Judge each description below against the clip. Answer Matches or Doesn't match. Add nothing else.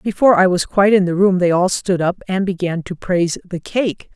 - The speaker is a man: Doesn't match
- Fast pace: Matches